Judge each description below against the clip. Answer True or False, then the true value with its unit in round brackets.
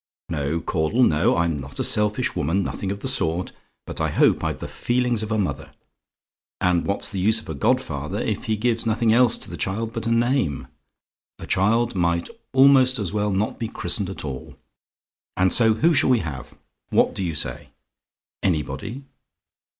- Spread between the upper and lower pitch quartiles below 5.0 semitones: False (5.5 semitones)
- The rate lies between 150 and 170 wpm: False (185 wpm)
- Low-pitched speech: True (105 Hz)